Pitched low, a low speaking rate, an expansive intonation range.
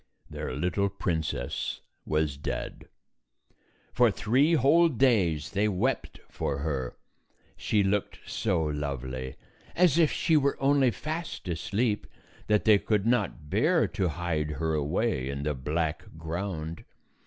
Yes: very low, 90 Hz; slow, 130 wpm; wide, 7.6 semitones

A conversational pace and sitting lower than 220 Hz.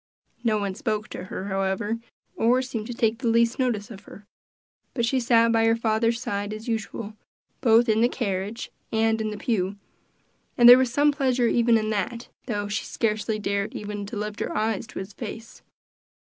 No: average, 190 wpm; high, 225 Hz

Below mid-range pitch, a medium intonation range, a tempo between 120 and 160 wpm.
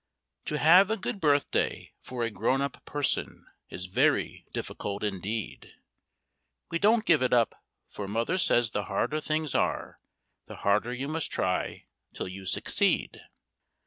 No: low, 130 Hz; wide, 7.0 semitones; average, 145 wpm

